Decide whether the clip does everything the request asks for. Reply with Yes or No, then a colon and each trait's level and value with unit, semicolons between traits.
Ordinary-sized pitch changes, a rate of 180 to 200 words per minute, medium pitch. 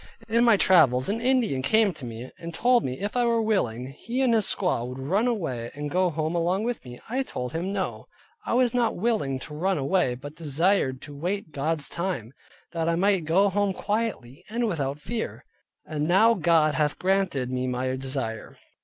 No: wide, 7.5 semitones; average, 195 wpm; medium, 170 Hz